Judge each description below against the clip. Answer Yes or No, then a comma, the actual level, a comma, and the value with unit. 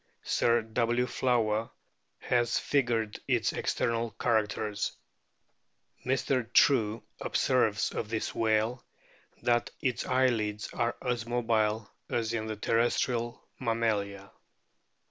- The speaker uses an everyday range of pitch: No, narrow, 1.9 semitones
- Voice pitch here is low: Yes, low, 115 Hz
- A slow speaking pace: Yes, slow, 110 wpm